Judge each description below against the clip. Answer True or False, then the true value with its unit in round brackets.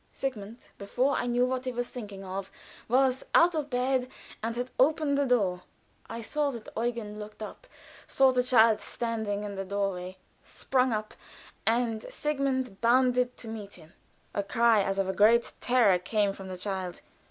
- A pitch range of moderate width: True (3.9 semitones)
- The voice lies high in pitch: True (230 Hz)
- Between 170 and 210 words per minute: True (175 wpm)